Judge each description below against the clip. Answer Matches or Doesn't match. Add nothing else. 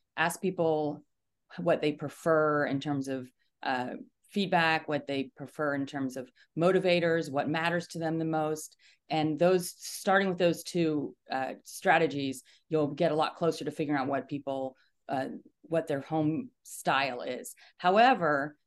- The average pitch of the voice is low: Doesn't match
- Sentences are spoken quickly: Doesn't match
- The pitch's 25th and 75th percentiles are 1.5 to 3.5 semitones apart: Matches